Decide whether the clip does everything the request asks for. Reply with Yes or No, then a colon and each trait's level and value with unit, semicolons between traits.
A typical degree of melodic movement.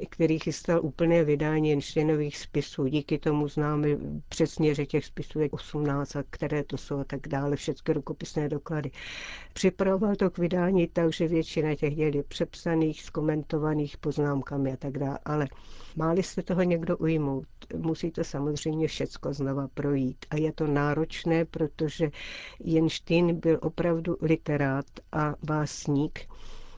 No: narrow, 2.1 semitones